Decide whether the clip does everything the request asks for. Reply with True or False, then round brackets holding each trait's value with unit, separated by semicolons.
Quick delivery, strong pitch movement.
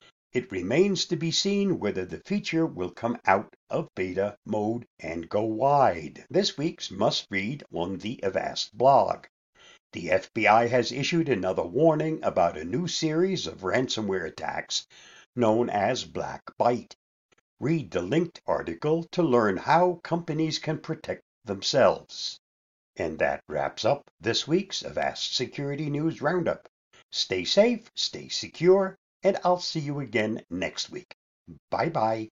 False (140 wpm; 7.6 semitones)